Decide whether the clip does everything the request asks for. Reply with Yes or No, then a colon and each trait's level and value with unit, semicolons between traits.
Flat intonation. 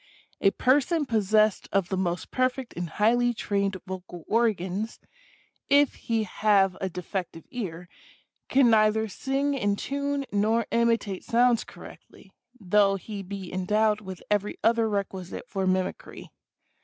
No: average, 3.6 semitones